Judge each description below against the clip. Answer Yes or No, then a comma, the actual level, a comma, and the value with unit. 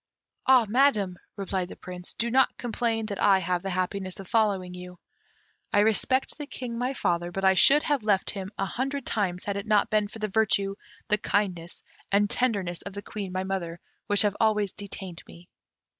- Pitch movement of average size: Yes, average, 3.0 semitones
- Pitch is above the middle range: Yes, high, 200 Hz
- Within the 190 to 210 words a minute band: Yes, average, 195 wpm